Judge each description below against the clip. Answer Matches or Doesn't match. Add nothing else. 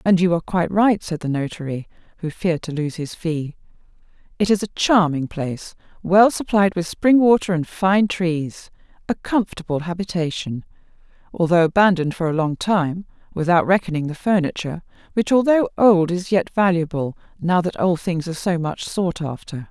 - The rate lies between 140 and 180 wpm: Matches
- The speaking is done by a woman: Matches